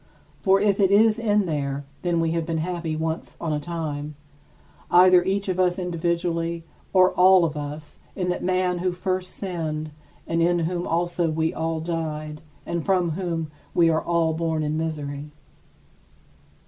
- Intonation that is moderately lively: No, narrow, 2.3 semitones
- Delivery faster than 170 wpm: No, average, 165 wpm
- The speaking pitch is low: No, medium, 170 Hz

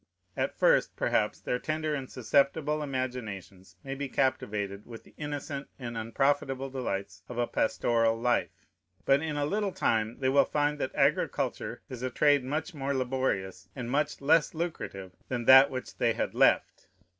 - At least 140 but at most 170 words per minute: Yes, average, 165 wpm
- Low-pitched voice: Yes, low, 130 Hz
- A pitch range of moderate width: Yes, average, 3.9 semitones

